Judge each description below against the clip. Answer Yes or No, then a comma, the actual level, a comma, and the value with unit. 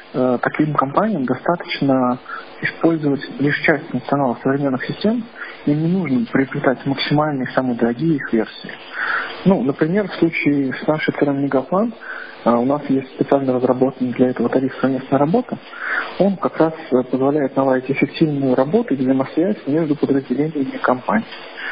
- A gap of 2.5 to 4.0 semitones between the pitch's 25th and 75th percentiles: Yes, average, 3.5 semitones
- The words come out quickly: No, average, 135 wpm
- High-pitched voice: No, medium, 140 Hz